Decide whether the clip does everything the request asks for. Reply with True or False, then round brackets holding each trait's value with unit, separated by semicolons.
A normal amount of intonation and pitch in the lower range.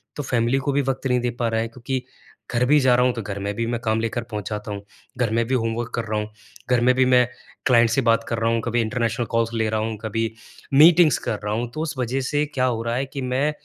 False (2.3 semitones; 120 Hz)